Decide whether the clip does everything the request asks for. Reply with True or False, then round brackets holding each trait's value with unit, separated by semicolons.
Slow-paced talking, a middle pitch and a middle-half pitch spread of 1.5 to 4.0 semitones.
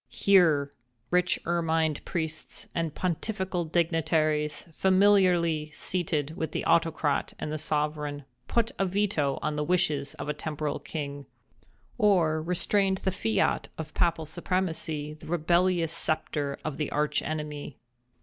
True (130 wpm; 160 Hz; 2.9 semitones)